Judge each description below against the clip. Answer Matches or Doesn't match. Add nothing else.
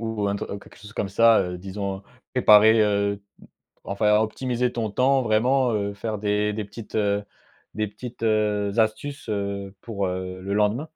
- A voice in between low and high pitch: Doesn't match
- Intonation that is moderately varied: Doesn't match